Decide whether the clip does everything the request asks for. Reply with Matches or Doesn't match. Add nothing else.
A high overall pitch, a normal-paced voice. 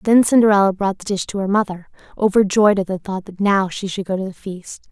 Doesn't match